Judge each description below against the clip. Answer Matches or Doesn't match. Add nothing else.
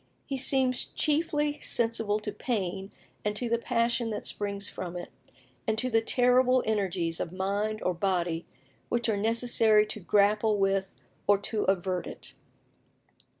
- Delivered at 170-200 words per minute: Doesn't match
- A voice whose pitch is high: Matches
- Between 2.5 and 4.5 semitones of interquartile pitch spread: Matches